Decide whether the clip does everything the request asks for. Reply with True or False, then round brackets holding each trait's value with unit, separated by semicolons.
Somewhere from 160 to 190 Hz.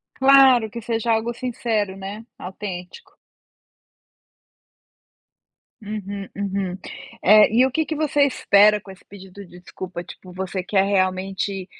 False (200 Hz)